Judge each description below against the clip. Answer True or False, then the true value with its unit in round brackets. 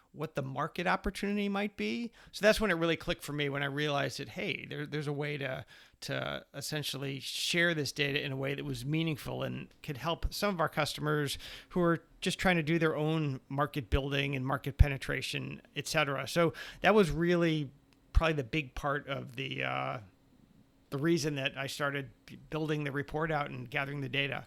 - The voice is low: False (145 Hz)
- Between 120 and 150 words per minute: False (200 wpm)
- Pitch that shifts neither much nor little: True (3.1 semitones)